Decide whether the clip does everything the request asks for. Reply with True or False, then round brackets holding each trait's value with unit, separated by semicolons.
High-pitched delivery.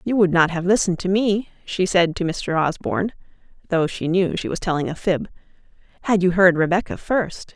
False (180 Hz)